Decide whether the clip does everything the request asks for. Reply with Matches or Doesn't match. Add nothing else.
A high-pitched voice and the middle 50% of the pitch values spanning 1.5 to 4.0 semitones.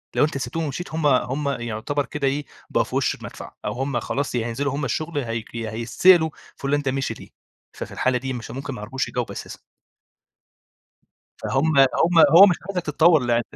Doesn't match